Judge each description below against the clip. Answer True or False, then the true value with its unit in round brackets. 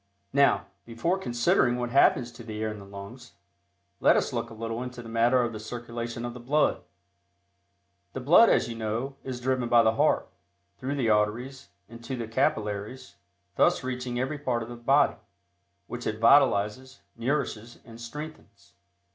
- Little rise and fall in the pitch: True (2.3 semitones)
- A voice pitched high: False (120 Hz)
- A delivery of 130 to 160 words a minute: False (170 wpm)